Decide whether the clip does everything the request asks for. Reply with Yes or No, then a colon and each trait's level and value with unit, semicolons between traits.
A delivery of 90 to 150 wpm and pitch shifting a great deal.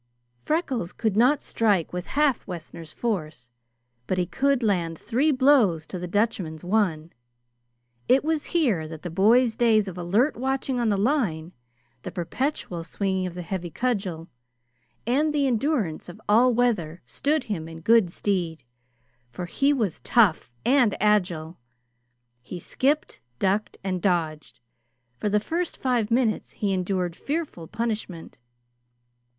Yes: average, 140 wpm; wide, 6.3 semitones